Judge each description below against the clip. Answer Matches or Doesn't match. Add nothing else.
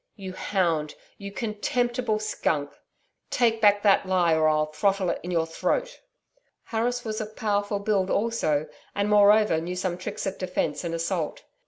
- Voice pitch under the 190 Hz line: Doesn't match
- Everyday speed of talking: Matches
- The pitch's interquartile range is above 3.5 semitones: Matches